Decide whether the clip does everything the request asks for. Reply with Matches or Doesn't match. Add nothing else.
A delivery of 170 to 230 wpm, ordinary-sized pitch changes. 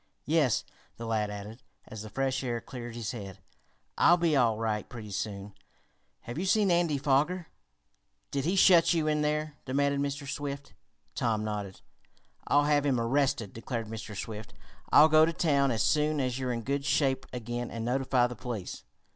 Matches